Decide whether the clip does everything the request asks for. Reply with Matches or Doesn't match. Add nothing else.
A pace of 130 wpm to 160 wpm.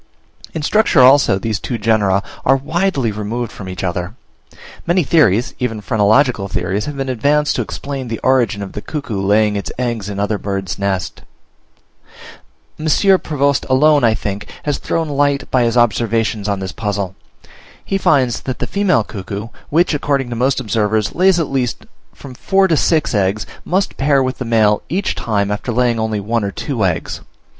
Doesn't match